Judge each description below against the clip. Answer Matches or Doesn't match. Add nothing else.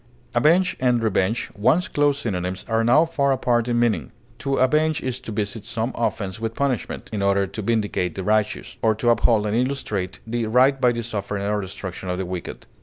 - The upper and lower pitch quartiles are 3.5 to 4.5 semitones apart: Matches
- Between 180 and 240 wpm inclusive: Matches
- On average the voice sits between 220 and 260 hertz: Doesn't match